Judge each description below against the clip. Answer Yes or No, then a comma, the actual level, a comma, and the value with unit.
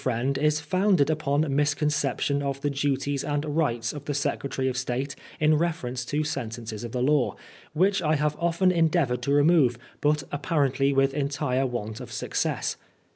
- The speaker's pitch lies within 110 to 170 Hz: Yes, medium, 140 Hz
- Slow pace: No, average, 165 wpm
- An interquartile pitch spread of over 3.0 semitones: No, narrow, 2.6 semitones